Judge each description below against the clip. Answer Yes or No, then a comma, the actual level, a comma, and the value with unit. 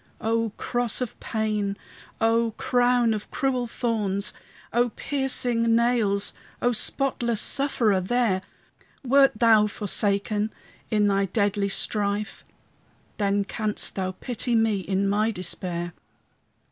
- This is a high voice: Yes, high, 220 Hz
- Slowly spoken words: Yes, slow, 110 wpm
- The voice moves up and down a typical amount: Yes, average, 3.1 semitones